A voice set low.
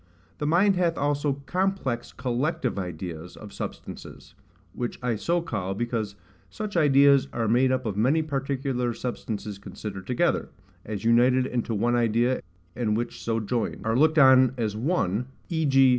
Yes: low, 125 Hz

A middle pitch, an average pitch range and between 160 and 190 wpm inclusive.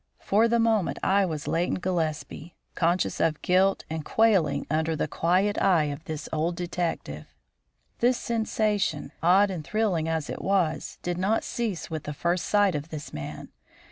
Yes: medium, 175 Hz; average, 4.1 semitones; average, 165 wpm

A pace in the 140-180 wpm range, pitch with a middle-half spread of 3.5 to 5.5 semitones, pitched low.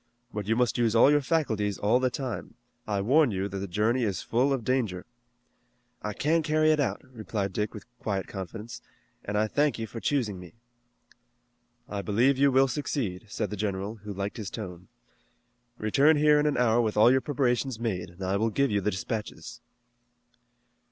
No: average, 190 wpm; average, 4.4 semitones; low, 115 Hz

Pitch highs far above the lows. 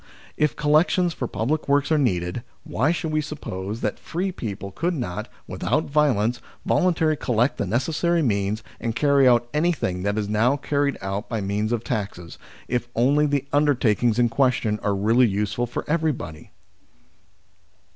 Yes: wide, 6.0 semitones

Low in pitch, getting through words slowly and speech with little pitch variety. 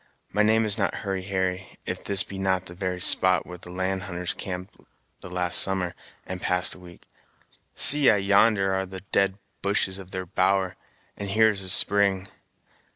No: very low, 95 Hz; average, 185 wpm; narrow, 1.4 semitones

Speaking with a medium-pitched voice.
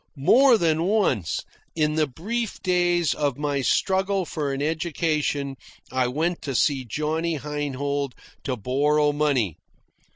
Yes: medium, 150 Hz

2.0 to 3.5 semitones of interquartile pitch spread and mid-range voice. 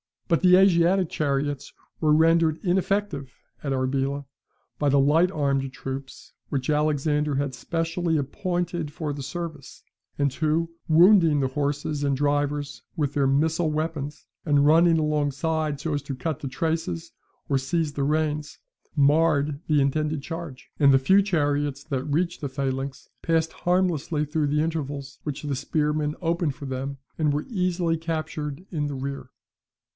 Yes: average, 2.7 semitones; medium, 150 Hz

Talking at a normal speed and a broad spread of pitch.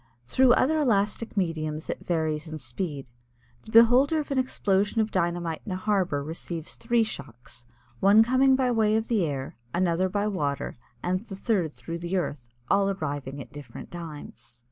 Yes: average, 170 wpm; wide, 6.3 semitones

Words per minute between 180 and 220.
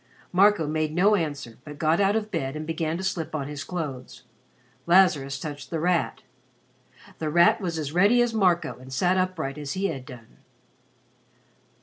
No: average, 170 wpm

